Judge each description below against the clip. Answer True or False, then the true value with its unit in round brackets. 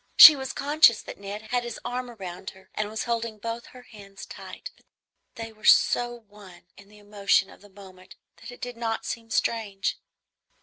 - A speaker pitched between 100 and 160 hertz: False (220 Hz)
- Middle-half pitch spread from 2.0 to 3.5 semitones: True (3.1 semitones)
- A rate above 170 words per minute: True (190 wpm)